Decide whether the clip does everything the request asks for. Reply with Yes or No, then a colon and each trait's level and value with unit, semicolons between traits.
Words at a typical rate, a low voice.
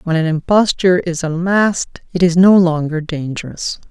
No: average, 155 wpm; medium, 170 Hz